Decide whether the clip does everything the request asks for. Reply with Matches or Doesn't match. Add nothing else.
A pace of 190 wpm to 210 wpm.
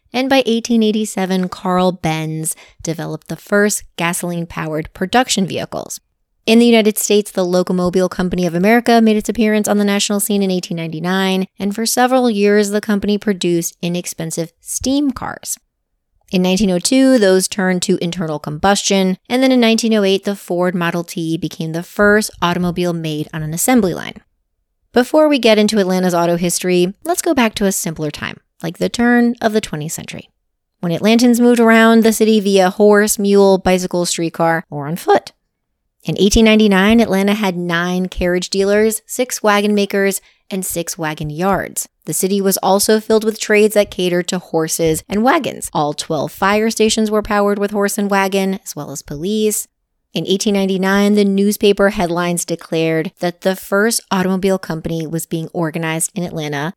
Doesn't match